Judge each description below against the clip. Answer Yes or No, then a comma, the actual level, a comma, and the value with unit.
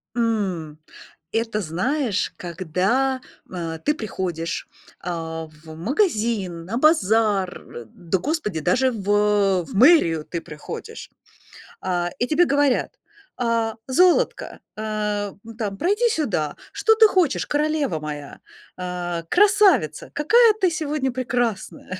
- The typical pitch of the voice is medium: No, high, 215 Hz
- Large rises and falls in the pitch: Yes, wide, 8.2 semitones